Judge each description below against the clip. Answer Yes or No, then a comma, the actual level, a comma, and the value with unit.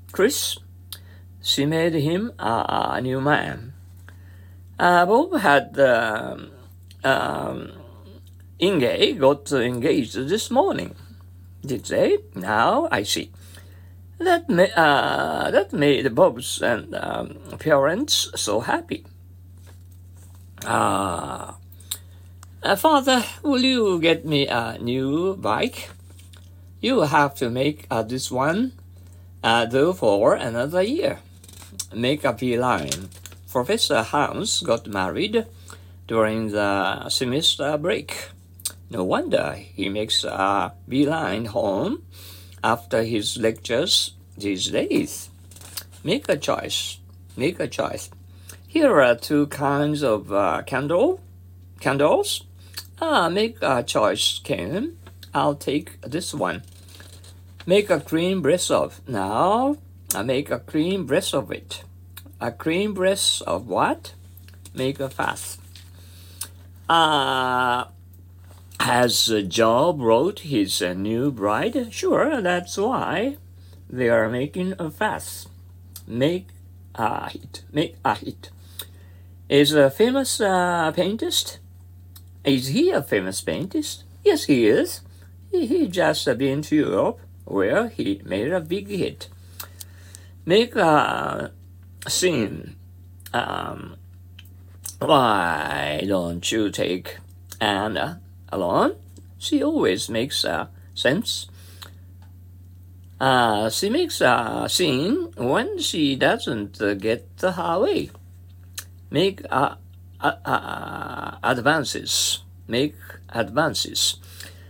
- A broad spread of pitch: Yes, wide, 6.1 semitones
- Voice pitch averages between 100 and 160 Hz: No, very low, 90 Hz